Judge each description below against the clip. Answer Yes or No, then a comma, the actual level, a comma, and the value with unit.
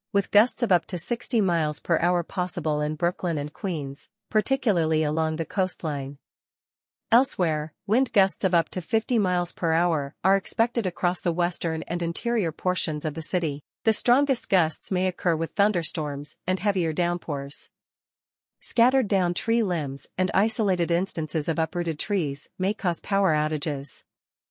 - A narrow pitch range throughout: No, average, 3.9 semitones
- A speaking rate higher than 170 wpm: No, average, 155 wpm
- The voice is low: No, medium, 175 Hz